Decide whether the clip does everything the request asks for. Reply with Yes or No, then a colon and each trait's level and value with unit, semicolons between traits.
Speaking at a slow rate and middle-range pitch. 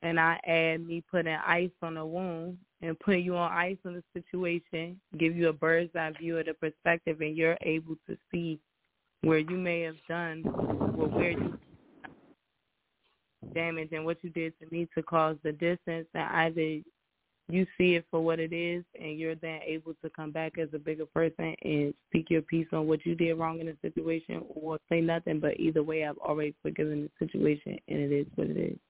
No: fast, 205 wpm; medium, 165 Hz